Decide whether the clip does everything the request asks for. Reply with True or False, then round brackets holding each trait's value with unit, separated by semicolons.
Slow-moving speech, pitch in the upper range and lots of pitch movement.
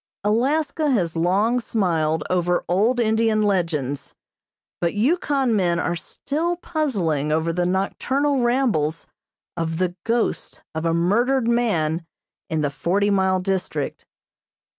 True (120 wpm; 195 Hz; 6.2 semitones)